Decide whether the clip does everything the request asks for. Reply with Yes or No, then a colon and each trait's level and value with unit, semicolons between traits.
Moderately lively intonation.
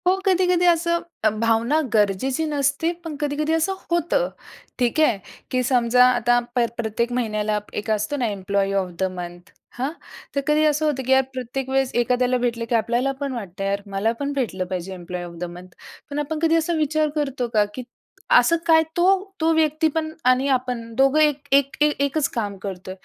No: wide, 5.8 semitones